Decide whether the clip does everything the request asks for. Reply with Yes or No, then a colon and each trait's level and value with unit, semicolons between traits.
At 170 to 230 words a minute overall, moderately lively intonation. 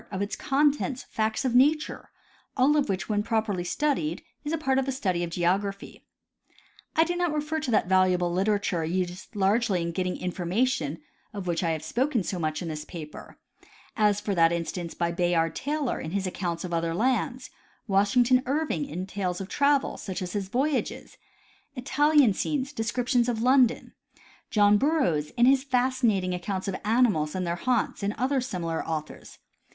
No: average, 175 wpm; wide, 6.5 semitones